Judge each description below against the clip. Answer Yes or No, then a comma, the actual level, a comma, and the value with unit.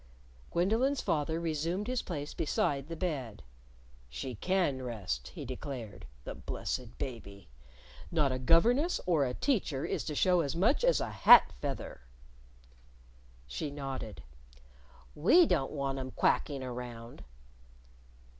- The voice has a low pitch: No, medium, 145 Hz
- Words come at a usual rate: No, slow, 130 wpm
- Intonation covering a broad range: Yes, wide, 5.7 semitones